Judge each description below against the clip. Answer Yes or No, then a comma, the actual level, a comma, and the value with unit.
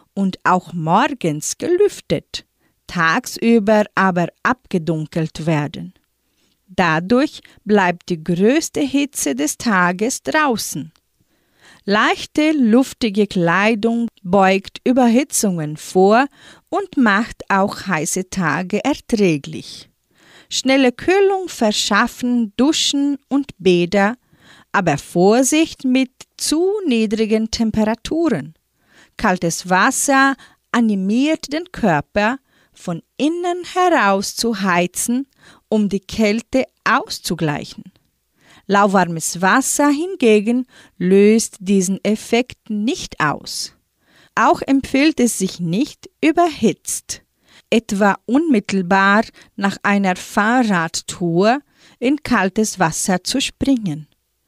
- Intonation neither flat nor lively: No, wide, 6.1 semitones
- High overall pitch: Yes, high, 220 Hz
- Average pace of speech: No, slow, 85 wpm